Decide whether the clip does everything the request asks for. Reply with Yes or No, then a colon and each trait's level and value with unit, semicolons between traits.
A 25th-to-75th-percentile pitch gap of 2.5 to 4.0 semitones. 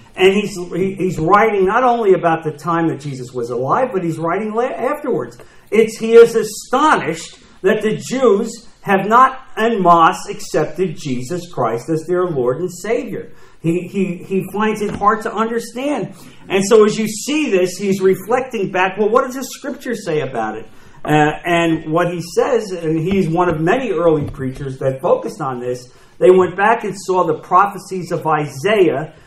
No: average, 4.9 semitones